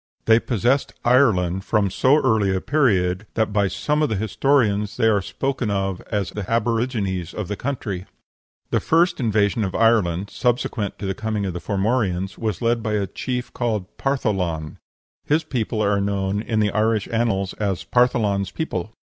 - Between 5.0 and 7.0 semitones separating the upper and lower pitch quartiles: No, average, 3.6 semitones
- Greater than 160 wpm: Yes, average, 170 wpm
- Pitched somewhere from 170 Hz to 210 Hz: No, low, 105 Hz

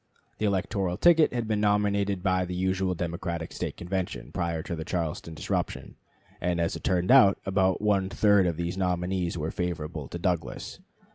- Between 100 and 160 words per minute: No, average, 185 wpm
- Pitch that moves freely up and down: No, narrow, 2.4 semitones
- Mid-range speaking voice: No, very low, 90 Hz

